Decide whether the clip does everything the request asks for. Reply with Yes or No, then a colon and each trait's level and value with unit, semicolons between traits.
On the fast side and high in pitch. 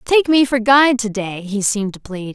Yes: fast, 255 wpm; high, 230 Hz